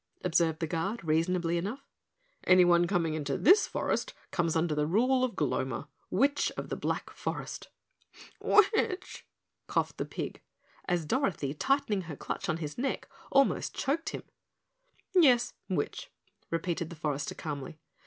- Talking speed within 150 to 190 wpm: No, average, 140 wpm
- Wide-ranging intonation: Yes, wide, 7.9 semitones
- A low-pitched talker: No, medium, 175 Hz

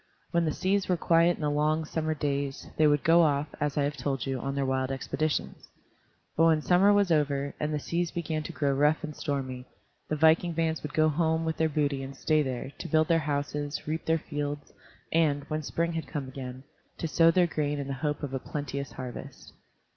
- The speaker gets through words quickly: Yes, fast, 220 wpm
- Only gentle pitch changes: Yes, narrow, 2.3 semitones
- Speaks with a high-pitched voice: No, medium, 150 Hz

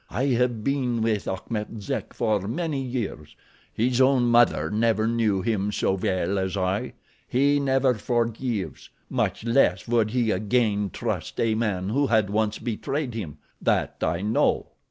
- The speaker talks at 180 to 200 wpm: No, average, 145 wpm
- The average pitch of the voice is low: Yes, low, 115 Hz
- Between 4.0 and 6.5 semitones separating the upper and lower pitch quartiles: No, average, 3.3 semitones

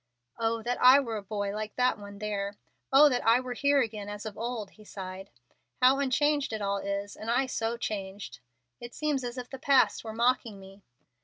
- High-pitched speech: Yes, high, 225 Hz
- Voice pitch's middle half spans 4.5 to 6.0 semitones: No, average, 3.8 semitones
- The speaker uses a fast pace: Yes, fast, 210 wpm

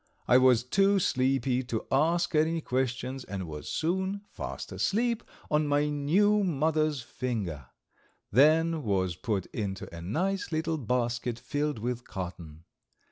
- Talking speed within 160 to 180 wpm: No, slow, 135 wpm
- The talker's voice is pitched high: No, low, 135 Hz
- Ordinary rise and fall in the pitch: No, wide, 5.9 semitones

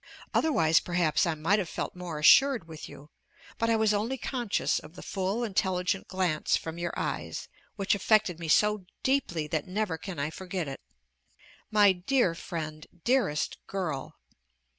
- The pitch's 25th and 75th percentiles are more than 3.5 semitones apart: Yes, average, 4.6 semitones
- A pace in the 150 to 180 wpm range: Yes, average, 160 wpm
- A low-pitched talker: No, medium, 185 Hz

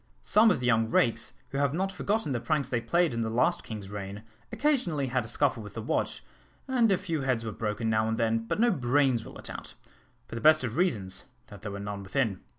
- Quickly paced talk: Yes, fast, 240 wpm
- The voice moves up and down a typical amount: No, wide, 5.8 semitones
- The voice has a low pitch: Yes, low, 120 Hz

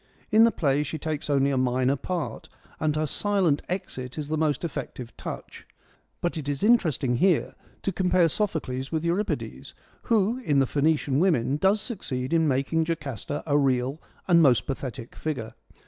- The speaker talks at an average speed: Yes, average, 165 wpm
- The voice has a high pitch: No, medium, 150 Hz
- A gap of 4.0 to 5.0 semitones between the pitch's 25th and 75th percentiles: Yes, average, 4.4 semitones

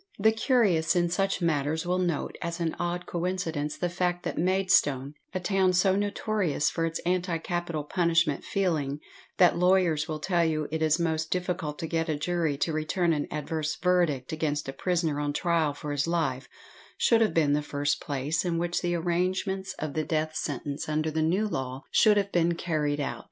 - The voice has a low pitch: No, medium, 165 Hz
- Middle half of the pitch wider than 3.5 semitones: No, average, 3.0 semitones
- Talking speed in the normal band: Yes, average, 190 wpm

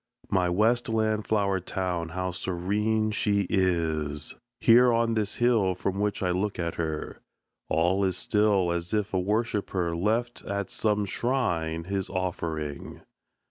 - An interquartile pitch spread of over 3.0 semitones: Yes, average, 3.6 semitones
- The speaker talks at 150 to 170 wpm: No, average, 140 wpm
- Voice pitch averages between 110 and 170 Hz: No, very low, 95 Hz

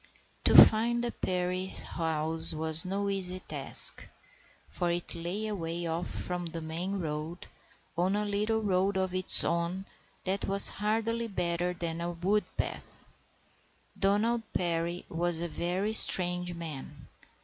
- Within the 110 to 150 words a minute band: Yes, average, 140 wpm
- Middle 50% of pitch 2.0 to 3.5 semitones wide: Yes, average, 2.8 semitones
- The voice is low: No, medium, 180 Hz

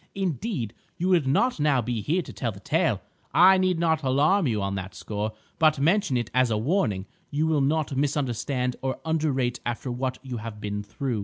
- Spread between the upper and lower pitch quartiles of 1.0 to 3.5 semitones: No, wide, 5.5 semitones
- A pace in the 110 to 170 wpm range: No, average, 200 wpm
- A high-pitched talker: No, low, 135 Hz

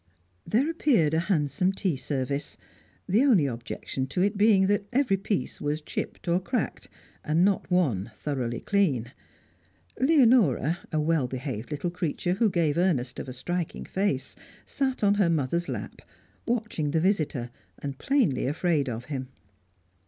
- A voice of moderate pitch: Yes, medium, 170 Hz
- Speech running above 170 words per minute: No, average, 150 wpm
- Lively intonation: Yes, wide, 6.4 semitones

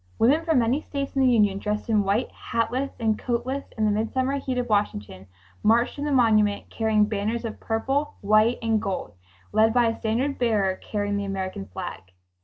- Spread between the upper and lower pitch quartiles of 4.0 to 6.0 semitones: No, average, 3.3 semitones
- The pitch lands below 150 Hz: No, high, 225 Hz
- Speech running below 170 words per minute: No, average, 190 wpm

